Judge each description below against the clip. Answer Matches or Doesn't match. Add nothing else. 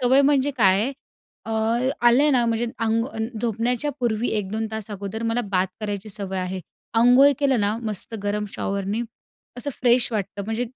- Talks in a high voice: Matches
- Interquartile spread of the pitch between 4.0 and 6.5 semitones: Doesn't match